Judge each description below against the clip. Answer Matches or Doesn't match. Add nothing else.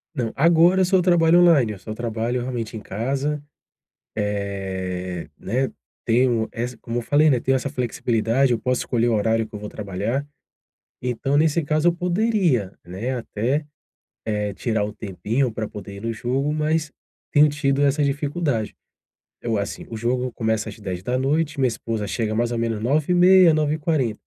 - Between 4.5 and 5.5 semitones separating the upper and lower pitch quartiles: Matches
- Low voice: Matches